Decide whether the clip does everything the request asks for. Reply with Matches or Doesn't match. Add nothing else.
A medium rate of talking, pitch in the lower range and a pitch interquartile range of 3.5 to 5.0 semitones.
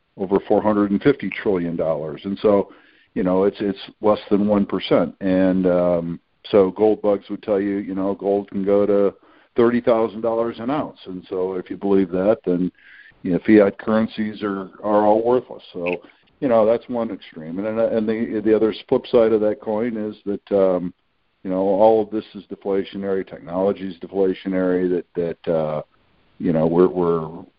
Doesn't match